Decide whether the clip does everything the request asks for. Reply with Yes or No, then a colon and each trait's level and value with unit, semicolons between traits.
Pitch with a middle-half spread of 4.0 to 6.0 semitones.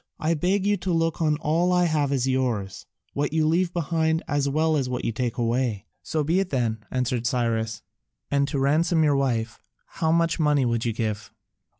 Yes: average, 5.1 semitones